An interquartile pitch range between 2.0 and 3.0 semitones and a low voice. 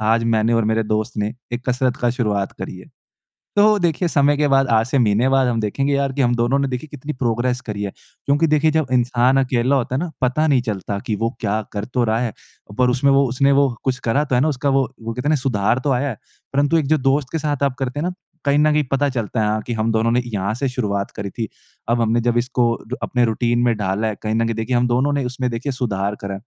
No: average, 3.6 semitones; low, 125 Hz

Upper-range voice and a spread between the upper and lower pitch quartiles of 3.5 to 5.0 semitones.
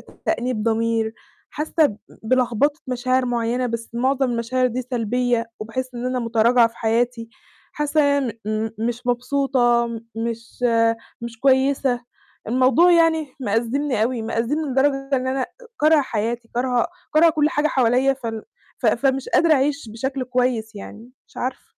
No: very high, 250 Hz; average, 2.8 semitones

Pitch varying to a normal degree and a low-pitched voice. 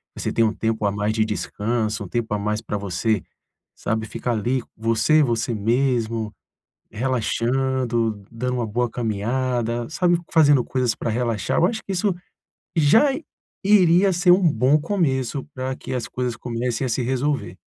Yes: average, 3.3 semitones; low, 120 Hz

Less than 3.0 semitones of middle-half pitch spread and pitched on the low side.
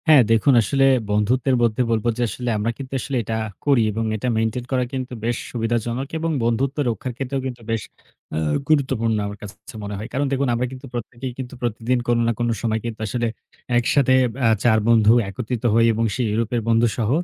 Yes: narrow, 2.5 semitones; low, 120 Hz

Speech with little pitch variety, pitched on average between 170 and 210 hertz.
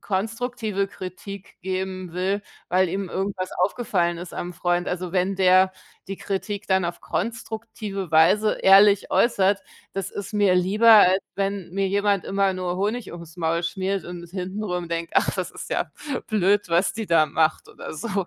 Yes: narrow, 2.2 semitones; high, 190 Hz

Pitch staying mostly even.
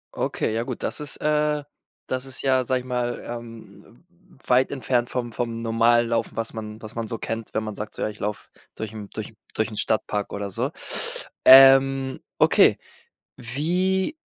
No: average, 3.3 semitones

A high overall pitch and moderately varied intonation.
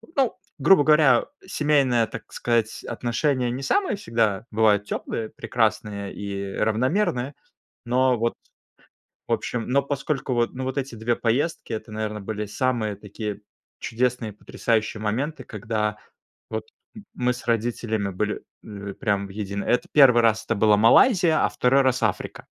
No: low, 115 Hz; average, 3.5 semitones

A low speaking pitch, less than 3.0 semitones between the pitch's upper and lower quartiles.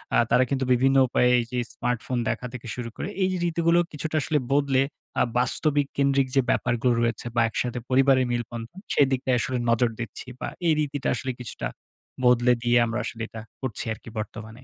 Yes: low, 125 Hz; narrow, 2.4 semitones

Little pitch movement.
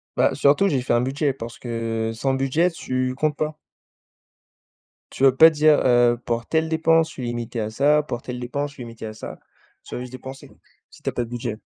No: average, 3.7 semitones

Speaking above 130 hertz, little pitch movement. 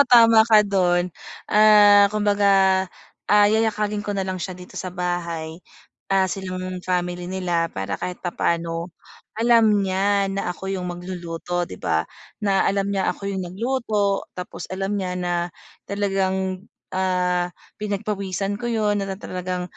Yes: high, 190 Hz; narrow, 2.2 semitones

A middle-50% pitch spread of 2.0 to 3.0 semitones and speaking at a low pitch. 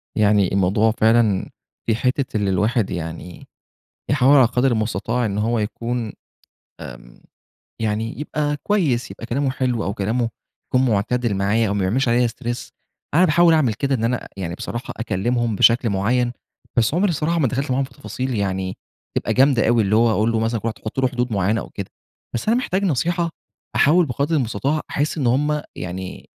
No: average, 4.2 semitones; low, 120 Hz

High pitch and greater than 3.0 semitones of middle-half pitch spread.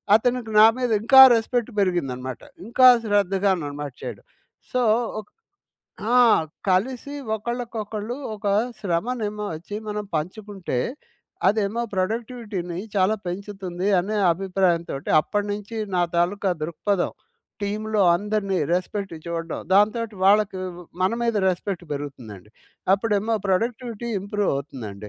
Yes: high, 200 Hz; average, 3.7 semitones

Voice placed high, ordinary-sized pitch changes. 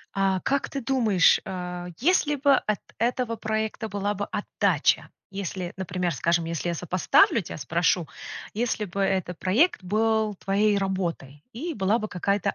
Yes: high, 195 Hz; average, 3.7 semitones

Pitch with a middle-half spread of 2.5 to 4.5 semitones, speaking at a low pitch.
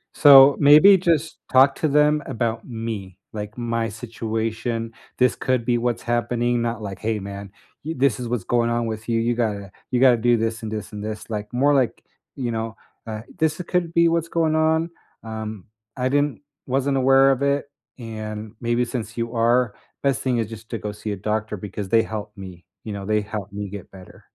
Yes: average, 3.6 semitones; low, 115 Hz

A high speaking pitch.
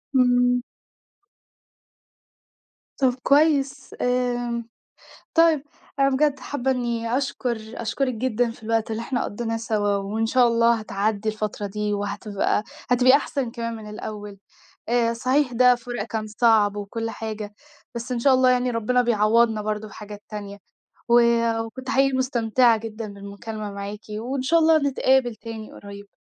Yes: high, 230 Hz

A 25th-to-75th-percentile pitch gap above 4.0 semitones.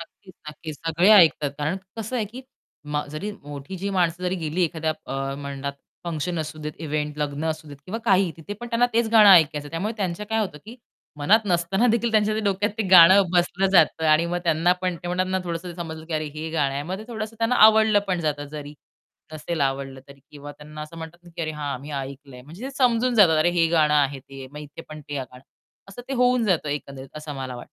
Yes: average, 4.7 semitones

